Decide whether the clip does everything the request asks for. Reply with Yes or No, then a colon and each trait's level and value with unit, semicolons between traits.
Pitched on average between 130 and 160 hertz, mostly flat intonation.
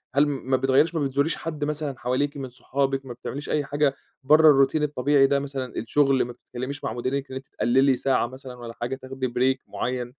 Yes: low, 135 Hz; narrow, 1.9 semitones